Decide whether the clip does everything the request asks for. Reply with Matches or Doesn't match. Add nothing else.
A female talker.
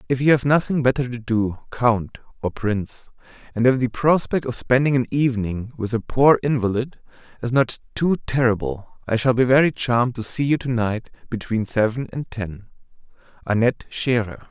Doesn't match